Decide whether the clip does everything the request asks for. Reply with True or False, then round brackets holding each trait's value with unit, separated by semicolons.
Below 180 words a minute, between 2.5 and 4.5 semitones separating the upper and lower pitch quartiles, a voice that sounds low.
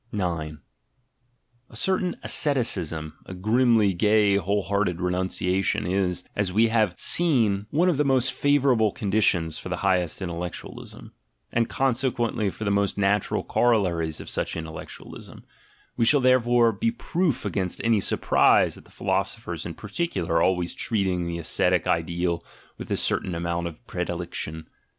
False (150 wpm; 5.1 semitones; 100 Hz)